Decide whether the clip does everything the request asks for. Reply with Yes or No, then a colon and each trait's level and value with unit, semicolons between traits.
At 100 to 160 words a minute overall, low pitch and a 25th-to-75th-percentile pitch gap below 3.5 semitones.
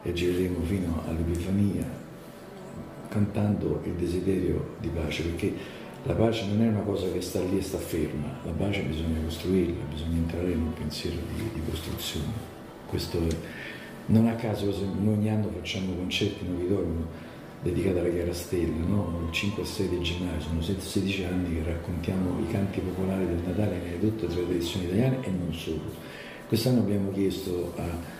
No: fast, 170 wpm; very low, 90 Hz; average, 3.1 semitones